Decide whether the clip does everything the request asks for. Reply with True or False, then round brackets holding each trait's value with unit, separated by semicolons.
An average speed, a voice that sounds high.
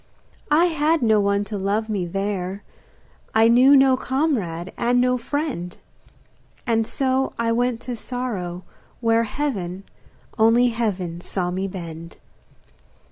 False (130 wpm; 225 Hz)